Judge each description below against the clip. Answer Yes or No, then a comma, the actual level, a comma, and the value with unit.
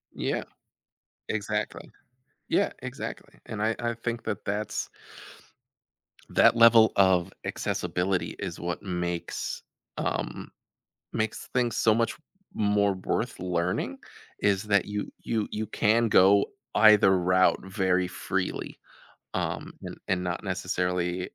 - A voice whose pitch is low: Yes, low, 100 Hz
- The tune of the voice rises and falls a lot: No, average, 3.1 semitones